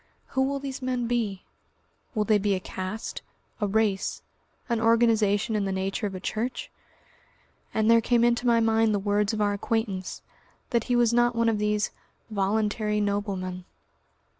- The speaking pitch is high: Yes, high, 215 Hz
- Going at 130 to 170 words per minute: Yes, average, 165 wpm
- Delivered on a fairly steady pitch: Yes, narrow, 2.3 semitones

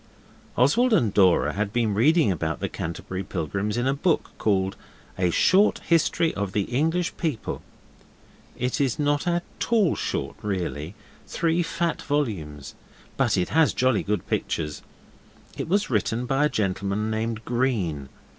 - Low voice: Yes, low, 115 Hz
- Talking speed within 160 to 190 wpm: No, average, 145 wpm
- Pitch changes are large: Yes, wide, 8.0 semitones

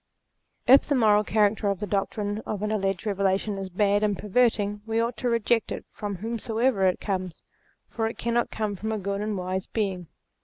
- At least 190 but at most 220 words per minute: Yes, average, 195 wpm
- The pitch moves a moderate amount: No, narrow, 2.2 semitones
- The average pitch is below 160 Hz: No, high, 210 Hz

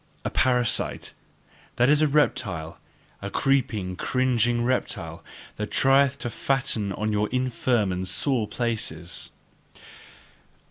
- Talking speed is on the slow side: Yes, slow, 110 wpm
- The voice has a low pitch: Yes, low, 120 Hz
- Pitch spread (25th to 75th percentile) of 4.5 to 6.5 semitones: No, average, 3.8 semitones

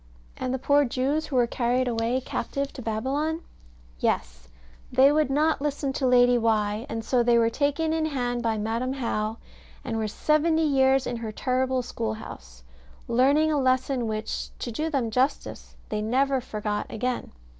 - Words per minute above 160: Yes, average, 170 wpm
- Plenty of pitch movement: No, average, 3.5 semitones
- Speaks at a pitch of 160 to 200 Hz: No, very high, 255 Hz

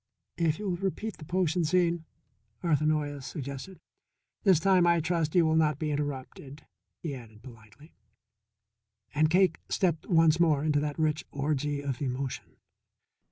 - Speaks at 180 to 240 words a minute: No, average, 150 wpm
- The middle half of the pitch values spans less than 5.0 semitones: Yes, average, 3.0 semitones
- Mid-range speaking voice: Yes, medium, 155 Hz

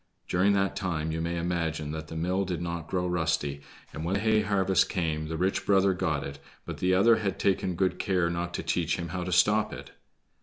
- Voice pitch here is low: Yes, very low, 90 Hz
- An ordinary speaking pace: No, fast, 220 wpm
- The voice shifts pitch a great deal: No, average, 2.9 semitones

